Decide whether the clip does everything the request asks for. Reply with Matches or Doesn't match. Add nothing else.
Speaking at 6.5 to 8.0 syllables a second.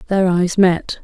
Doesn't match